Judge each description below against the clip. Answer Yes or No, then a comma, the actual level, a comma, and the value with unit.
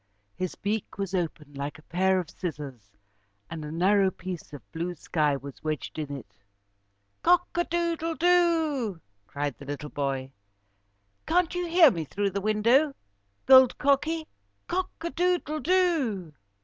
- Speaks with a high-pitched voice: Yes, high, 195 Hz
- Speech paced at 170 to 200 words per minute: No, average, 150 wpm